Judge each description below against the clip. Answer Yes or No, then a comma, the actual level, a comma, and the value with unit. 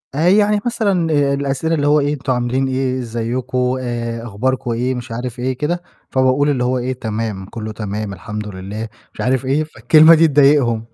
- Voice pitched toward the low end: Yes, low, 130 Hz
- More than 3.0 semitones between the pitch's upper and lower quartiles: Yes, average, 3.8 semitones